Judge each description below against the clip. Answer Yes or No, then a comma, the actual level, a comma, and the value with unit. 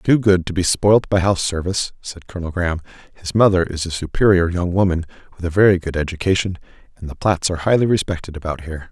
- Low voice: Yes, very low, 90 Hz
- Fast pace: Yes, fast, 210 wpm